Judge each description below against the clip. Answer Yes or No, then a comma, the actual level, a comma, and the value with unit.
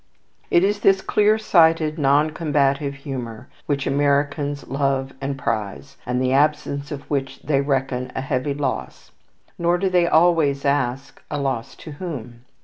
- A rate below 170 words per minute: Yes, average, 150 wpm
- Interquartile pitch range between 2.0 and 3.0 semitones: Yes, narrow, 2.5 semitones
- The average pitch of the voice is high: No, medium, 140 Hz